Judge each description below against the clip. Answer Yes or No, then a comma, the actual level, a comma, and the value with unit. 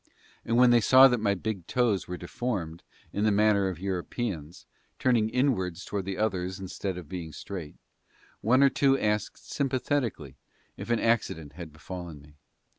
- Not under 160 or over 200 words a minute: Yes, average, 165 wpm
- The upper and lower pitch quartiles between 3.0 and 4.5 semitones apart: No, average, 5.1 semitones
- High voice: No, low, 100 Hz